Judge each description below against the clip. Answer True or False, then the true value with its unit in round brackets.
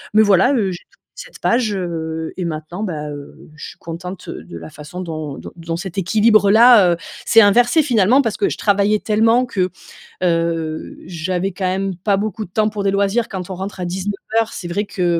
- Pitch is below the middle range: False (190 Hz)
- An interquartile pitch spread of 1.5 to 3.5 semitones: False (3.9 semitones)